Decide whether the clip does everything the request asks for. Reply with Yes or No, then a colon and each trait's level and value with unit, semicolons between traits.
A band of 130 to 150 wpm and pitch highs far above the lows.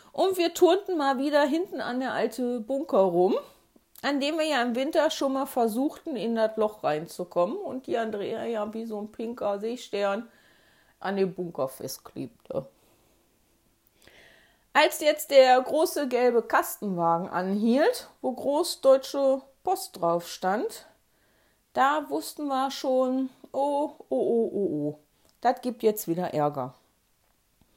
Yes: average, 135 wpm; wide, 6.7 semitones